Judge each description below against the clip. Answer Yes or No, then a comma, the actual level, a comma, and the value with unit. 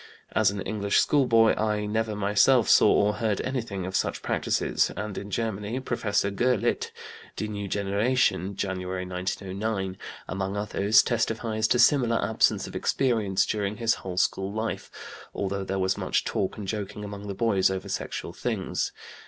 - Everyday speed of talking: Yes, average, 155 wpm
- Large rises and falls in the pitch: No, narrow, 2.5 semitones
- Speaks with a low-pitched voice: Yes, low, 105 Hz